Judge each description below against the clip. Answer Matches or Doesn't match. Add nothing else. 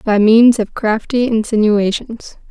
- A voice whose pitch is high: Matches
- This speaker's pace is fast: Doesn't match